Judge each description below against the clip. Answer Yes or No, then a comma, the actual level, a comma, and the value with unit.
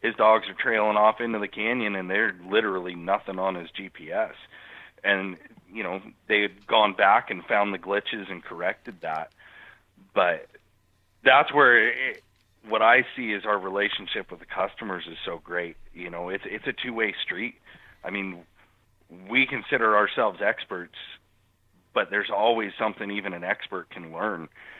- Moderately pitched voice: No, low, 100 Hz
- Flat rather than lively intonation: Yes, narrow, 2.0 semitones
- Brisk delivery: No, average, 170 wpm